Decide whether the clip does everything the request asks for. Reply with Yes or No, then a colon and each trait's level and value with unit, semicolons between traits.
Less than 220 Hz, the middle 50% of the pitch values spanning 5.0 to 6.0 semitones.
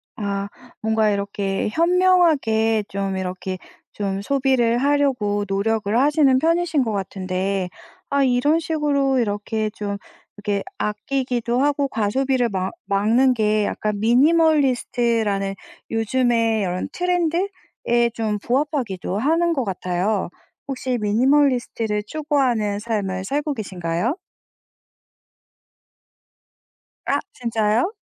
No: high, 230 Hz; average, 5.3 semitones